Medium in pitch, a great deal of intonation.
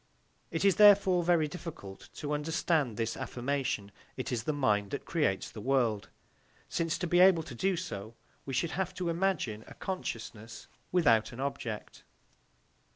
Yes: medium, 145 Hz; wide, 7.3 semitones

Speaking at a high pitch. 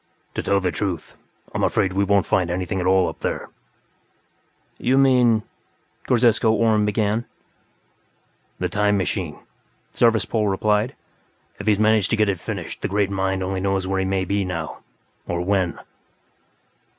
No: low, 100 Hz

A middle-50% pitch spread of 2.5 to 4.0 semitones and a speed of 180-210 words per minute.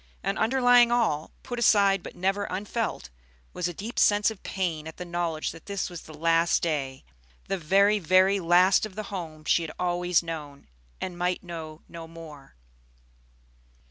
No: average, 3.5 semitones; average, 170 wpm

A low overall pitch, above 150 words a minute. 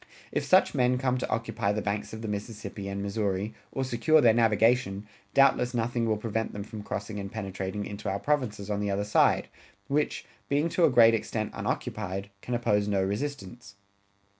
Yes: low, 110 Hz; average, 185 wpm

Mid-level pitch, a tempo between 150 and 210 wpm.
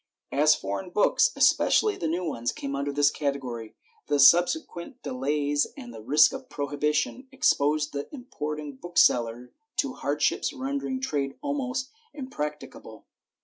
No: medium, 150 Hz; slow, 135 wpm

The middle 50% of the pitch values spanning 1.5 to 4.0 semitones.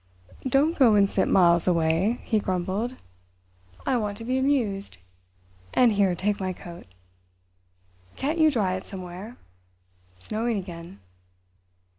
No: average, 5.2 semitones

